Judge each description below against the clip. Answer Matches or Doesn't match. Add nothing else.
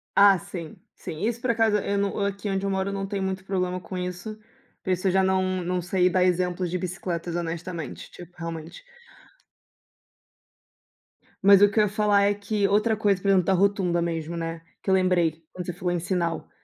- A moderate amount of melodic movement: Doesn't match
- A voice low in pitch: Doesn't match